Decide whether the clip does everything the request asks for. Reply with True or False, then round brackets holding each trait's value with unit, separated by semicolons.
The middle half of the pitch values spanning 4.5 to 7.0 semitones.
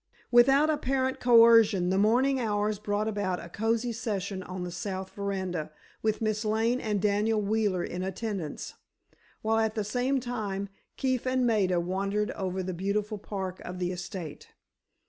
False (3.3 semitones)